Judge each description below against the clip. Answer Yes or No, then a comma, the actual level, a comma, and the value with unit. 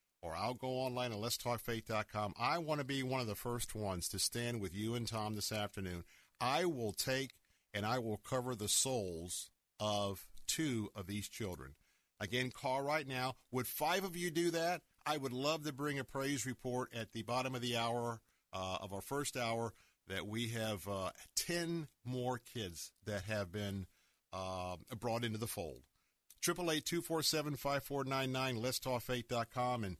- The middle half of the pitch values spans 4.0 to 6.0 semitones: Yes, average, 4.4 semitones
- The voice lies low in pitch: Yes, low, 120 Hz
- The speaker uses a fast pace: No, average, 170 wpm